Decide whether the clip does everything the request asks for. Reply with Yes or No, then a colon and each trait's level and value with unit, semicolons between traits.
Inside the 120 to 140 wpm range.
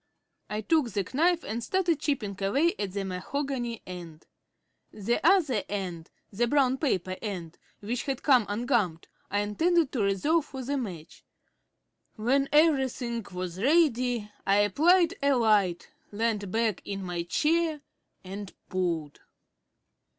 Yes: slow, 135 wpm